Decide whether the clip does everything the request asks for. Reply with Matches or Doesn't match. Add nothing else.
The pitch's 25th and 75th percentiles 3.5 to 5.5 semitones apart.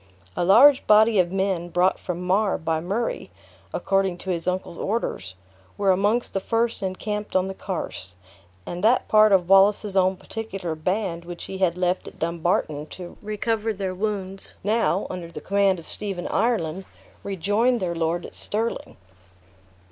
Doesn't match